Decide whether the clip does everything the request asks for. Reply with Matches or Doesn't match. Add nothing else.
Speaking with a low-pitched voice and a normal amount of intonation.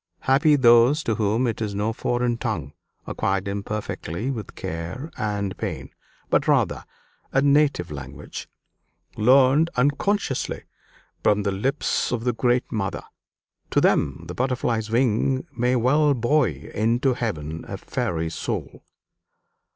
Matches